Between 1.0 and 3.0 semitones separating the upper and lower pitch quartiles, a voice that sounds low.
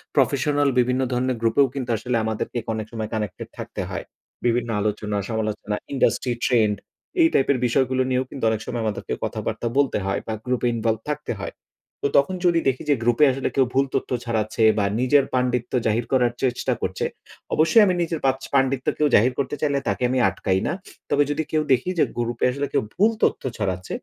No: average, 3.7 semitones; low, 125 Hz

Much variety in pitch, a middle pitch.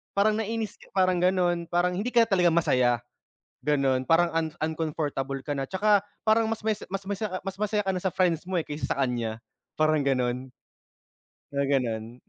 Yes: wide, 6.2 semitones; medium, 165 Hz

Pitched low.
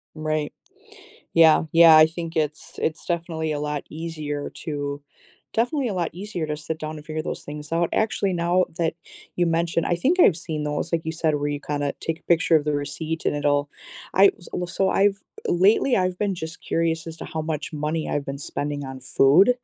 No: medium, 160 Hz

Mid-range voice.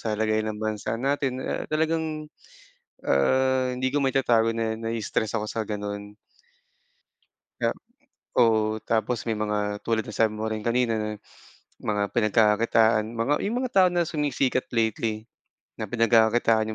No: low, 115 Hz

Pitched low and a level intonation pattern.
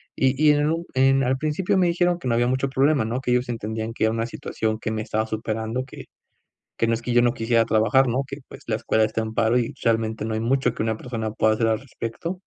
No: low, 115 Hz; average, 3.2 semitones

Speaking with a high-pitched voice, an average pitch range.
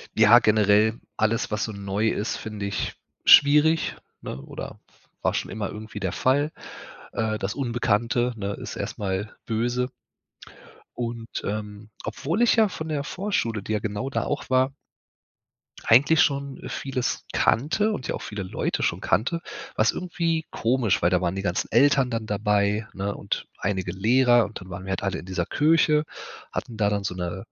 No: low, 110 Hz; average, 4.7 semitones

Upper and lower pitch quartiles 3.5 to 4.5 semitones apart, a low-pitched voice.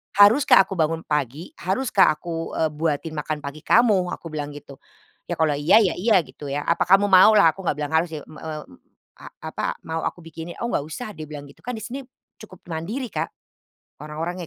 No: average, 4.2 semitones; medium, 165 Hz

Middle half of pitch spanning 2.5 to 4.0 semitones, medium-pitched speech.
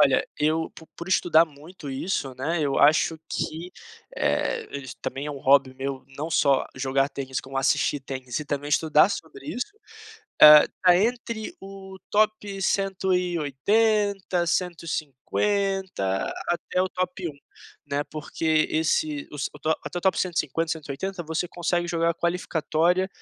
No: average, 4.7 semitones; medium, 165 Hz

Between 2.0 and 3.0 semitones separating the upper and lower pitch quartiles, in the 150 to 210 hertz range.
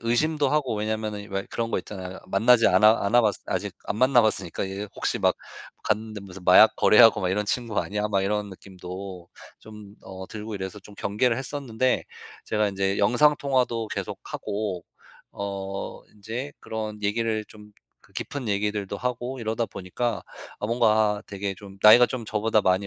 No: average, 2.7 semitones; low, 105 Hz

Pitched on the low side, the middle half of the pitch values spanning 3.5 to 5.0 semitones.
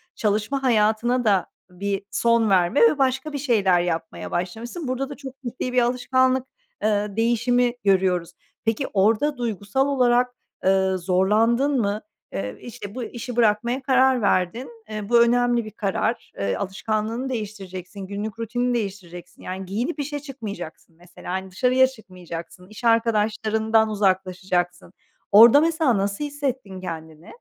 No: high, 220 Hz; average, 4.5 semitones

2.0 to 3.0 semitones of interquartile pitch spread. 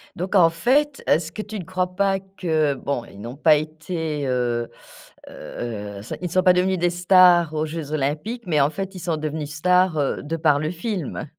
No: average, 3.7 semitones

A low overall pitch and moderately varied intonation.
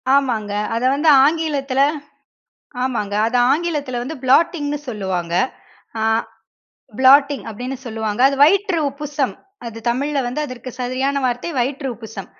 No: very high, 265 Hz; average, 3.5 semitones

